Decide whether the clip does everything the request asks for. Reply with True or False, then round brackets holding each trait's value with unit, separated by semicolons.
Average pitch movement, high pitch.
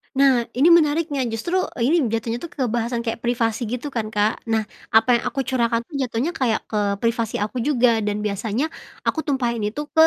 True (3.3 semitones; 235 Hz)